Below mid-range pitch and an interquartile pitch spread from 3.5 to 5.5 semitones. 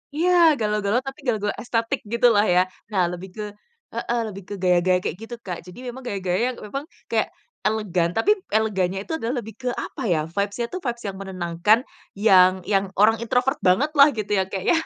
No: high, 210 Hz; average, 4.2 semitones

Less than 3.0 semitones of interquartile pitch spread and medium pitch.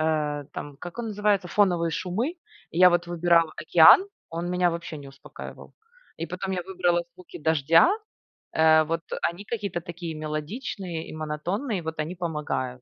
Yes: narrow, 2.5 semitones; medium, 170 Hz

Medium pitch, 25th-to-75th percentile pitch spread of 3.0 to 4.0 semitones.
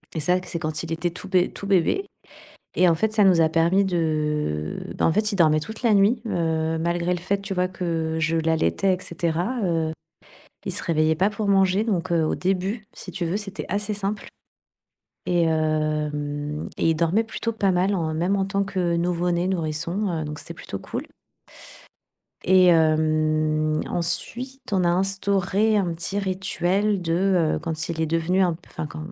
Yes: medium, 175 Hz; average, 3.4 semitones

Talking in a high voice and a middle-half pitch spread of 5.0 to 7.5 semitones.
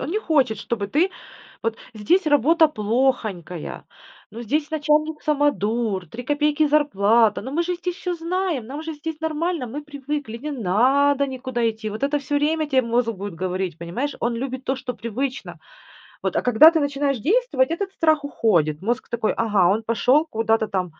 Yes: very high, 265 Hz; wide, 5.4 semitones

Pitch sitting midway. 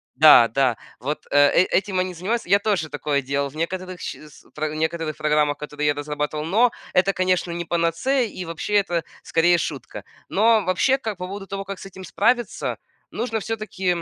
Yes: medium, 175 Hz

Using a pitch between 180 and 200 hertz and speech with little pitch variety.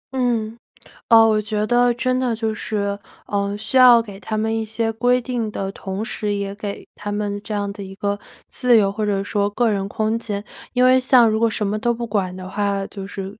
No: high, 215 Hz; narrow, 2.3 semitones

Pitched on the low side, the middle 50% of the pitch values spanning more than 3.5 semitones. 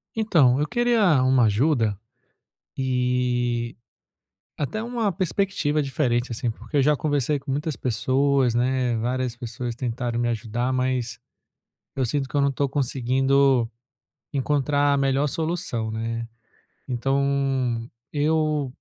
No: low, 130 Hz; average, 3.1 semitones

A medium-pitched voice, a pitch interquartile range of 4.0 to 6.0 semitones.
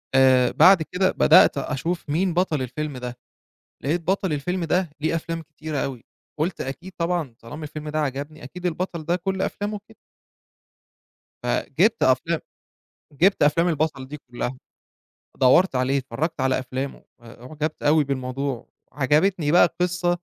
Yes: medium, 155 Hz; average, 4.7 semitones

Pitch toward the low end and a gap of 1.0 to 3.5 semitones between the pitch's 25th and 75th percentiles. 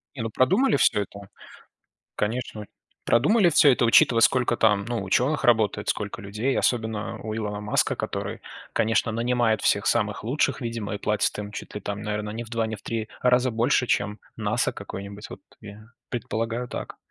Yes: low, 110 Hz; narrow, 2.6 semitones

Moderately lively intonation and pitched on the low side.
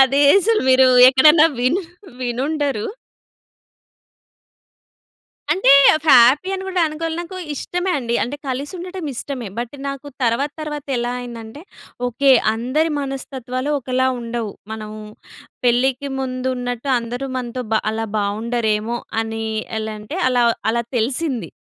No: average, 3.6 semitones; very high, 255 Hz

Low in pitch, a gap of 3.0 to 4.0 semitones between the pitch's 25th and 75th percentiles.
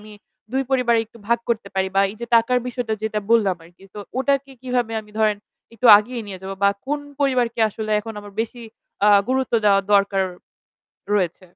No: high, 225 Hz; average, 3.4 semitones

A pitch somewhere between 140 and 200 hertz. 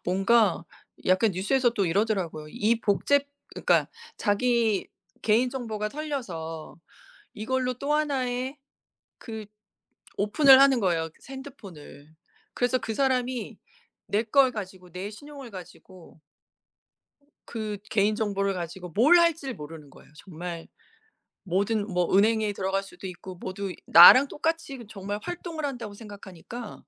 No: high, 215 Hz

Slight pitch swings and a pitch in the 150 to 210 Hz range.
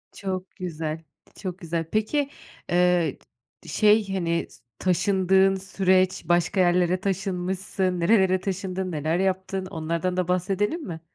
Yes: narrow, 1.7 semitones; medium, 185 Hz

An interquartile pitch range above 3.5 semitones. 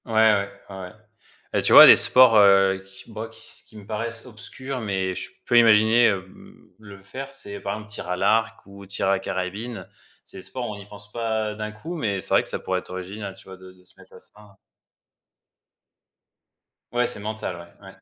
No: narrow, 2.6 semitones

